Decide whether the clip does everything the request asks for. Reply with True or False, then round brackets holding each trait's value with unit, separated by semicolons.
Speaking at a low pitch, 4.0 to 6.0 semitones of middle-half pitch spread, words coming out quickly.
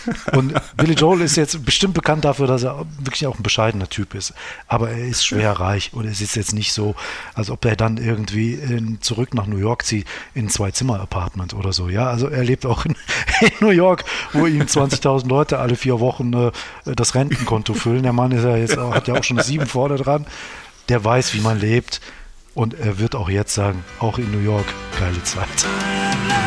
True (120 Hz; 4.4 semitones; 215 wpm)